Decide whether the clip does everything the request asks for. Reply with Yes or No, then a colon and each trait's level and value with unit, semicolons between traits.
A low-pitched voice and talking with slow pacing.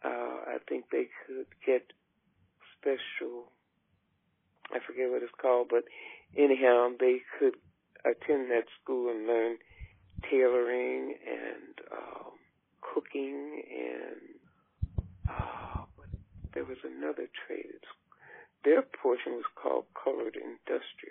Yes: low, 125 Hz; slow, 105 wpm